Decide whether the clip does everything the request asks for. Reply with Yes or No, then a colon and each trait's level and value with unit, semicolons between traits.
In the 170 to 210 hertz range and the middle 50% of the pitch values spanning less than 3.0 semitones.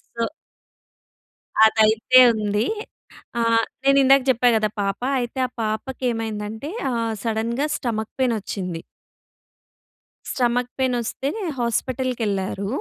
No: high, 230 Hz; narrow, 2.6 semitones